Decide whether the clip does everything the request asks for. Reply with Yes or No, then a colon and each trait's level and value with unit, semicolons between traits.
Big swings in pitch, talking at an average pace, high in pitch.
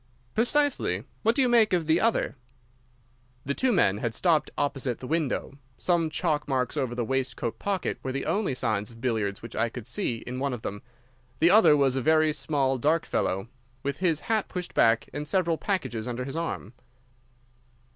No: wide, 6.0 semitones; average, 185 wpm; medium, 140 Hz